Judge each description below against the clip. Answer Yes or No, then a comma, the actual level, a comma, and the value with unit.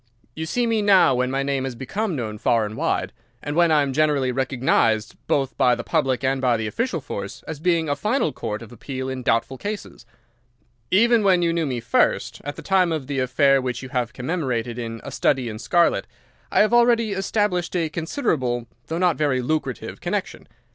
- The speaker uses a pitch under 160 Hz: Yes, medium, 140 Hz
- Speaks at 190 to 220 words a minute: Yes, fast, 205 wpm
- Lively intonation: Yes, wide, 5.8 semitones